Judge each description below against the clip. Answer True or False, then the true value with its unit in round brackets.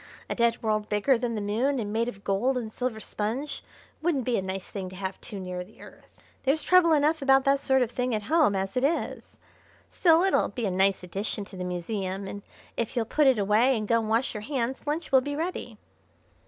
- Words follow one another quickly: True (230 wpm)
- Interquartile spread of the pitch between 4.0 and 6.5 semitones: True (5.0 semitones)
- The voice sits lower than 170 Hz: False (230 Hz)